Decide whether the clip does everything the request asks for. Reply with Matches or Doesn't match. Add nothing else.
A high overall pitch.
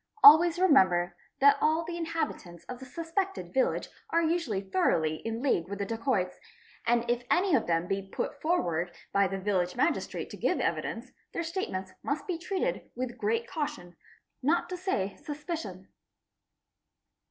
Matches